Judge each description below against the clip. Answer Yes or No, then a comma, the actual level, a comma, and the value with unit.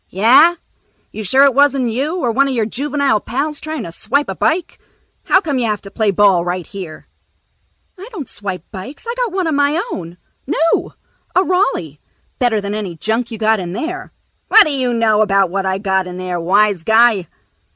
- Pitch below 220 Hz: No, high, 225 Hz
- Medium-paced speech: Yes, average, 195 wpm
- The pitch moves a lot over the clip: Yes, wide, 6.6 semitones